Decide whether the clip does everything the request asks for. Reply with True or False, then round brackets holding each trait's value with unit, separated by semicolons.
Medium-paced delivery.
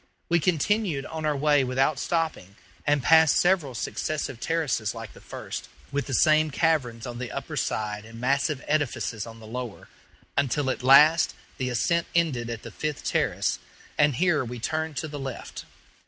True (170 wpm)